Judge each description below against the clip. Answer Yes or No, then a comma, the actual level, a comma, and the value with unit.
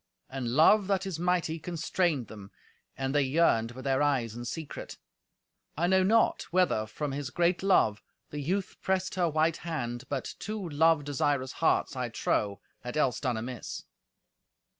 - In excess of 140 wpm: Yes, average, 160 wpm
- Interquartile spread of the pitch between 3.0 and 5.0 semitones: No, wide, 5.5 semitones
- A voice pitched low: No, medium, 145 Hz